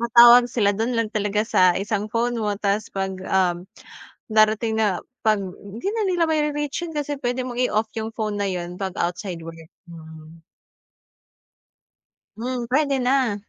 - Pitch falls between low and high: No, high, 215 Hz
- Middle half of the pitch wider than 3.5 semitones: Yes, average, 4.2 semitones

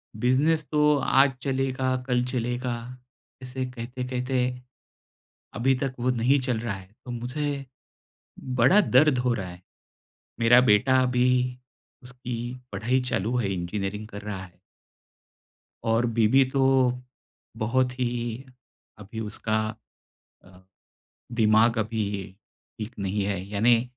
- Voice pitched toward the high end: No, low, 125 Hz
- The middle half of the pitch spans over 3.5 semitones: No, average, 2.9 semitones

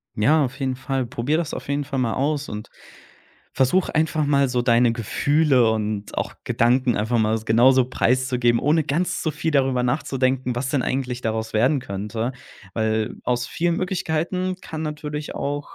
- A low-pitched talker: Yes, low, 130 Hz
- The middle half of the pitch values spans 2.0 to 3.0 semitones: No, average, 3.9 semitones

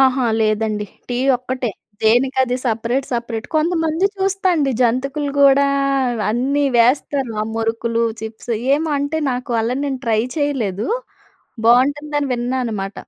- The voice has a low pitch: No, very high, 255 Hz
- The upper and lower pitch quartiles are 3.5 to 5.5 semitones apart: Yes, average, 3.8 semitones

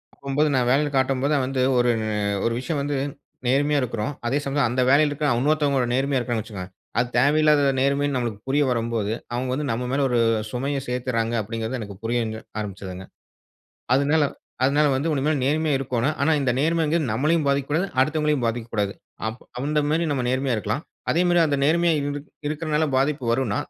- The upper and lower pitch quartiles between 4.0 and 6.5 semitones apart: No, average, 3.5 semitones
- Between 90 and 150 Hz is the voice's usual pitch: Yes, low, 135 Hz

